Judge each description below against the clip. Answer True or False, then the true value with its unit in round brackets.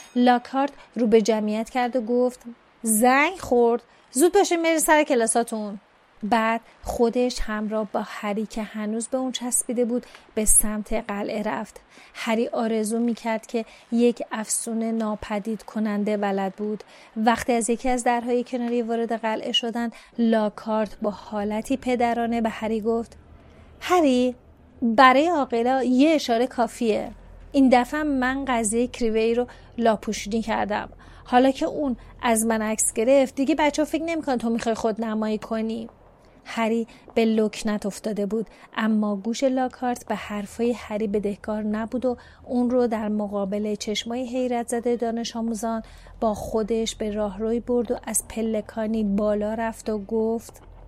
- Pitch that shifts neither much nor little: False (2.2 semitones)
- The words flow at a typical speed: True (140 wpm)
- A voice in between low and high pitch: False (230 Hz)